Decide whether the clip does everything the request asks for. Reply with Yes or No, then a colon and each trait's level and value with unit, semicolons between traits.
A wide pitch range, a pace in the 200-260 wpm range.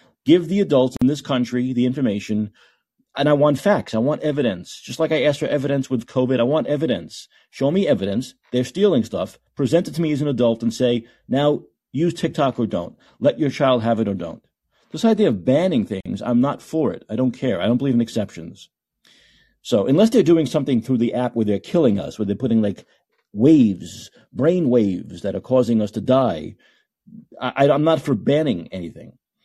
No: average, 4.2 semitones; fast, 205 wpm